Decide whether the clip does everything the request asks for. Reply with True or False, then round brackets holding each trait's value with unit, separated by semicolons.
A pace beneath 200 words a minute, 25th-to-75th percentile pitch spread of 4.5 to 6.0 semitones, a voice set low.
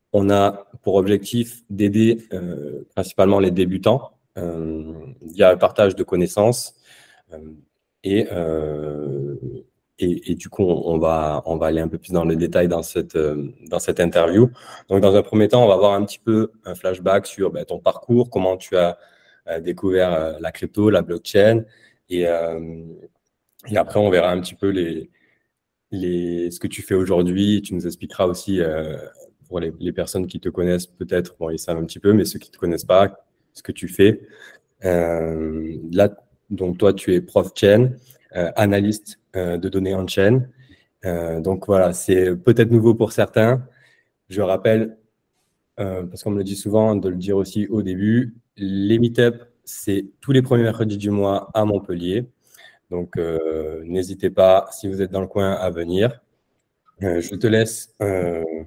False (185 wpm; 3.7 semitones; 95 Hz)